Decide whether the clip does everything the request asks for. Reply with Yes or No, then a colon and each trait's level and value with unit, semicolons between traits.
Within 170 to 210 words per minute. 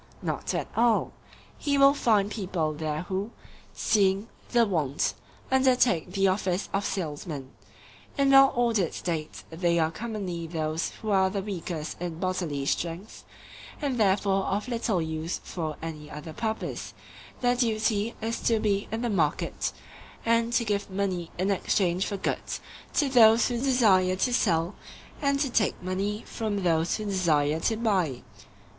No: average, 150 wpm